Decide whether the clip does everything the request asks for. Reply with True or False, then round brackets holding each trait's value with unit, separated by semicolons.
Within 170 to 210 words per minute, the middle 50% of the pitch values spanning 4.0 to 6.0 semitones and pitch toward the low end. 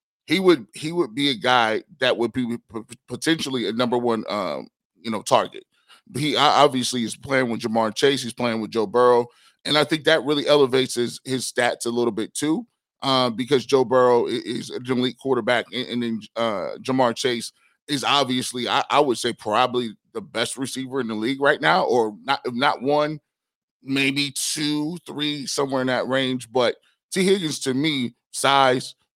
False (190 wpm; 3.0 semitones; 130 Hz)